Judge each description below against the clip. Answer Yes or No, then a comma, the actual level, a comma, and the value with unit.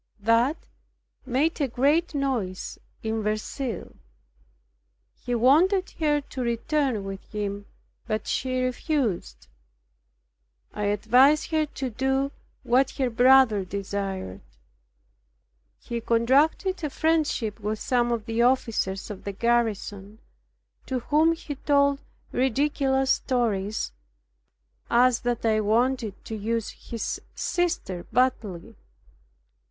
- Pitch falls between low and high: No, high, 240 Hz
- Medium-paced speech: No, slow, 105 wpm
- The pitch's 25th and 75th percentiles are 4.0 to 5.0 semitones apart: Yes, average, 4.4 semitones